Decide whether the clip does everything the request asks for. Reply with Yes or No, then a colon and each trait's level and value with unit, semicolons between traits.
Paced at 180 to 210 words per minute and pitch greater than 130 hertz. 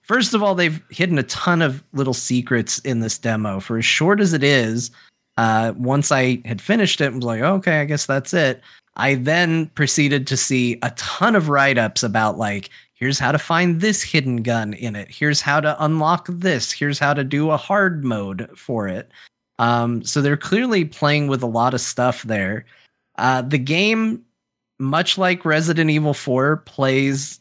Yes: average, 195 wpm; medium, 140 Hz